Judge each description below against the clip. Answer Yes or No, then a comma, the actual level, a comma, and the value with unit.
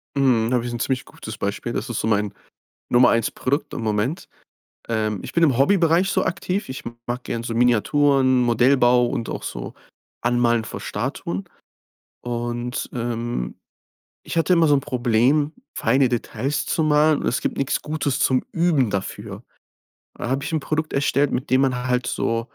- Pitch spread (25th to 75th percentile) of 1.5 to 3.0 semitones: No, average, 3.4 semitones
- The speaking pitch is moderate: No, low, 125 Hz